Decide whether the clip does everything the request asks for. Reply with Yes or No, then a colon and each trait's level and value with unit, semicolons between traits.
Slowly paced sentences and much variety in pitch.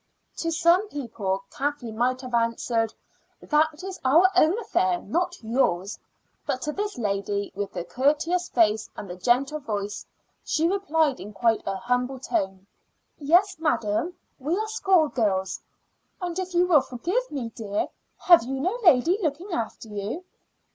No: average, 150 wpm; wide, 7.8 semitones